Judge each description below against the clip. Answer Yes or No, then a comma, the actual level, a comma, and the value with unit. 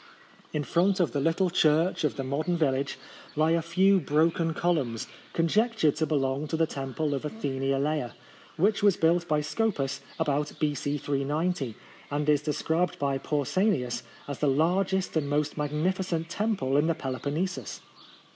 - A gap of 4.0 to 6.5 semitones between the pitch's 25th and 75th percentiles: No, average, 3.5 semitones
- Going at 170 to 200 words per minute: No, average, 155 wpm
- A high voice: No, medium, 155 Hz